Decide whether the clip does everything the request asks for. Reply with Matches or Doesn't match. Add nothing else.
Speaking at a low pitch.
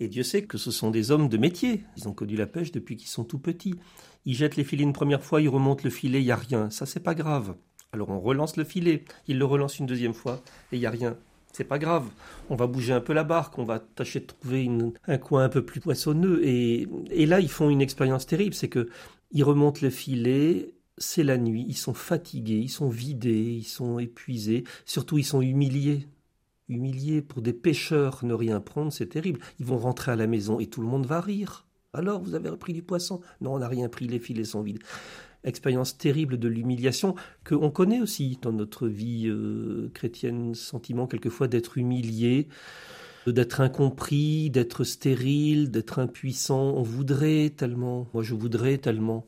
Matches